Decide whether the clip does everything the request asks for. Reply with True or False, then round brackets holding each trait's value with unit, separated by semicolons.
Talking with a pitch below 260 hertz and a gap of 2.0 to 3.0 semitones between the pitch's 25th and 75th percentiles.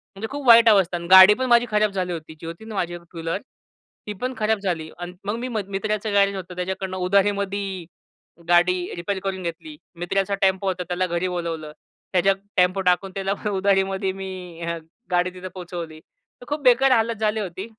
True (190 Hz; 2.6 semitones)